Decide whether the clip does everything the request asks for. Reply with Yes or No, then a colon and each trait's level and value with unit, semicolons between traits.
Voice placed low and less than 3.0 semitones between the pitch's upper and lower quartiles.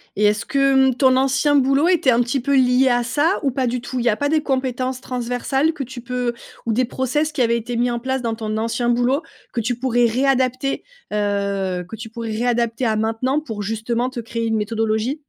No: high, 245 Hz; narrow, 2.6 semitones